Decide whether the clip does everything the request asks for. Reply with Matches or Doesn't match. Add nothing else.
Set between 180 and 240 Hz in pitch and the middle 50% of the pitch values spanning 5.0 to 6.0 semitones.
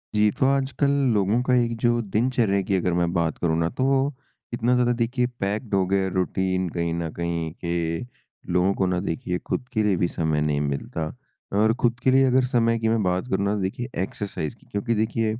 Doesn't match